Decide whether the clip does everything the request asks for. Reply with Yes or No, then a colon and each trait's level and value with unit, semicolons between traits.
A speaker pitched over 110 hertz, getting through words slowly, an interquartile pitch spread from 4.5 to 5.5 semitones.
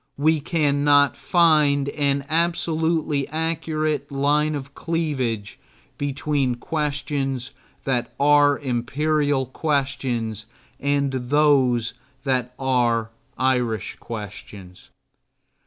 No: medium, 140 Hz; slow, 80 wpm; average, 3.0 semitones